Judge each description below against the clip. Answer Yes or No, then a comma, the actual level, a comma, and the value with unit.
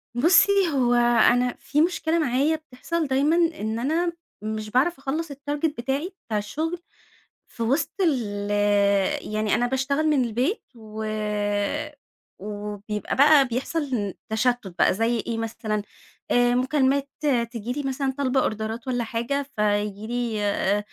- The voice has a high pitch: Yes, very high, 250 Hz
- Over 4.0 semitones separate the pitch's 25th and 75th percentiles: Yes, average, 4.7 semitones